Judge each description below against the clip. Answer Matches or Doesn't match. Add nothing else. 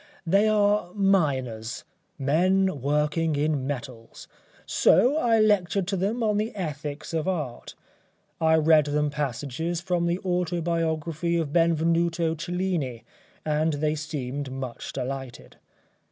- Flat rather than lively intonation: Doesn't match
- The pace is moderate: Doesn't match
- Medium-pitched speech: Matches